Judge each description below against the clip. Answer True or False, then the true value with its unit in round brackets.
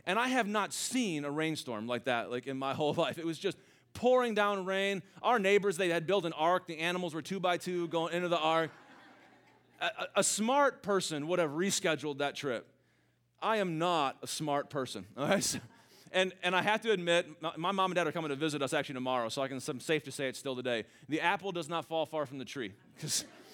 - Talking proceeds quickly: True (235 wpm)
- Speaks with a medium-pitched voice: True (170 Hz)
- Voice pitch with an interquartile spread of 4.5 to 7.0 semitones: True (5.0 semitones)